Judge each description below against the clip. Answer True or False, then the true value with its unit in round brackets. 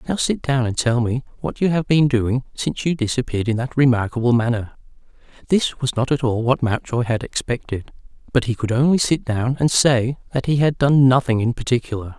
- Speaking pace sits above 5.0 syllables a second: True (5.5 syllables/s)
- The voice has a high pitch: False (125 Hz)